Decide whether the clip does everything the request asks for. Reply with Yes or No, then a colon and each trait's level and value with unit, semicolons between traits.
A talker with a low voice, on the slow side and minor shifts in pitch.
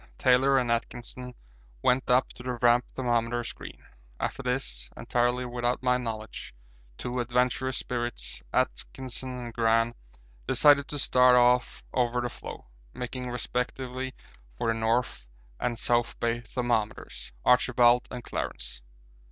Yes: low, 125 Hz; slow, 125 wpm; narrow, 1.1 semitones